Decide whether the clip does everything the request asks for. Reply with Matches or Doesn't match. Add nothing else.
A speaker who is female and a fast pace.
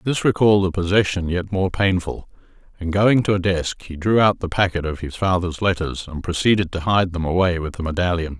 Doesn't match